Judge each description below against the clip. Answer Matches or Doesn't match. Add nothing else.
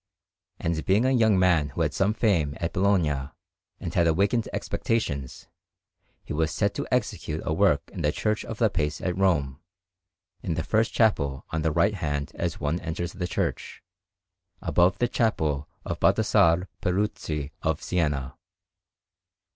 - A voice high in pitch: Doesn't match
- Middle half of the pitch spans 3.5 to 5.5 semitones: Matches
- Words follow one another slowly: Doesn't match